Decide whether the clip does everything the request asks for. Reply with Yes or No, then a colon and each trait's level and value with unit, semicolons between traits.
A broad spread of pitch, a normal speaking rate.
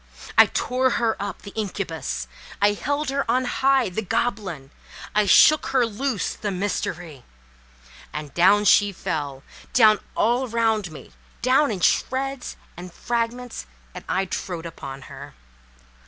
No: wide, 6.1 semitones; slow, 115 wpm